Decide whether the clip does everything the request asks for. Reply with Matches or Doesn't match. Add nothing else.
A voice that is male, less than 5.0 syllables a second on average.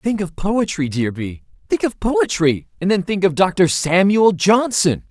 Matches